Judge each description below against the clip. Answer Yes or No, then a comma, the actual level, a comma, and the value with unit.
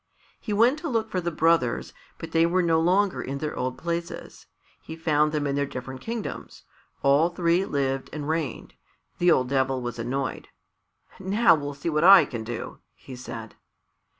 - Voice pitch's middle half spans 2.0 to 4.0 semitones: No, average, 4.6 semitones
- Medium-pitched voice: Yes, medium, 155 Hz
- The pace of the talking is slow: No, average, 180 wpm